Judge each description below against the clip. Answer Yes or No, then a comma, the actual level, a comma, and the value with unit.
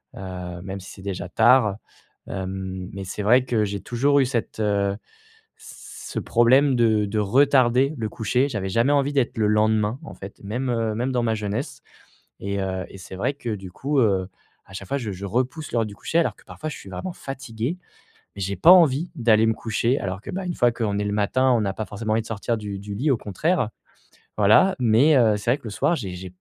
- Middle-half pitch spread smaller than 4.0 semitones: No, average, 4.6 semitones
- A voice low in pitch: Yes, low, 110 Hz